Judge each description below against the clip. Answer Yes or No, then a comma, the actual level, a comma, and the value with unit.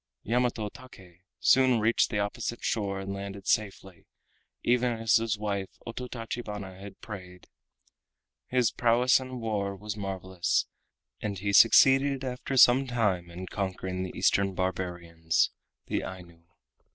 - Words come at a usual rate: No, slow, 125 wpm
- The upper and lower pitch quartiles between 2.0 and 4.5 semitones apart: Yes, average, 4.1 semitones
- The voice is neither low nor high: No, low, 100 Hz